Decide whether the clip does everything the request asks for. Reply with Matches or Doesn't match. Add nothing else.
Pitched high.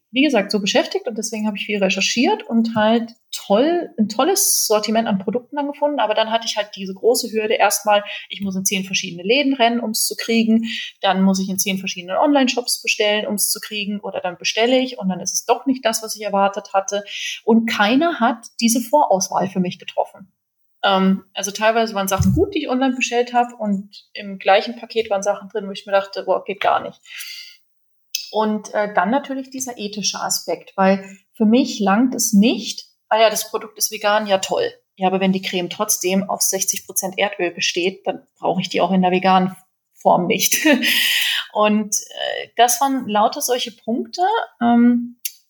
Matches